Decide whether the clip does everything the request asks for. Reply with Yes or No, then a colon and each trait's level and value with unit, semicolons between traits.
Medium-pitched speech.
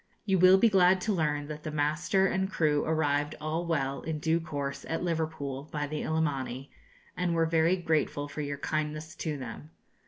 Yes: medium, 155 Hz